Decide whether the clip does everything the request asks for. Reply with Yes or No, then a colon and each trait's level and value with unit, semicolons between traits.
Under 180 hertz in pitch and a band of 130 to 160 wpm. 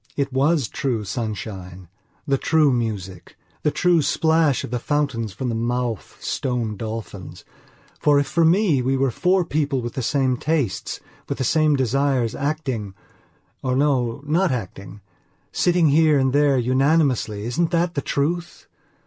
Yes: low, 135 Hz; average, 150 wpm